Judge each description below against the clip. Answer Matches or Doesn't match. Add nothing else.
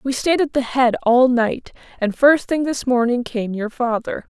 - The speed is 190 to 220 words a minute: Matches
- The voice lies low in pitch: Doesn't match